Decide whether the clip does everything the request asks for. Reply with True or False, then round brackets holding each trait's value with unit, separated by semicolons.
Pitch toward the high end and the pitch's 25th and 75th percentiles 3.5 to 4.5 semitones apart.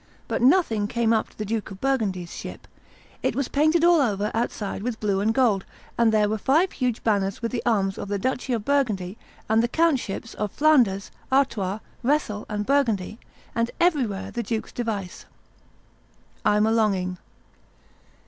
True (225 Hz; 4.2 semitones)